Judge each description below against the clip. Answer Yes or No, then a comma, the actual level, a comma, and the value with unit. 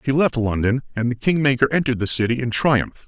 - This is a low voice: Yes, low, 125 Hz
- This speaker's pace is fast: Yes, fast, 215 wpm